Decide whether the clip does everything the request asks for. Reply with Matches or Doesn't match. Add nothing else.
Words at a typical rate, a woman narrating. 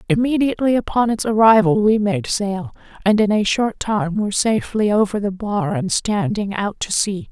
Matches